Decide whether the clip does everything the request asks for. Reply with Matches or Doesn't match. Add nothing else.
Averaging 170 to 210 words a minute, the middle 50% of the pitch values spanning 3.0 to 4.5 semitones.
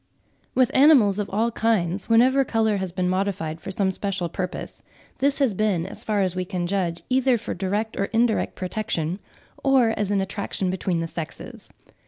Matches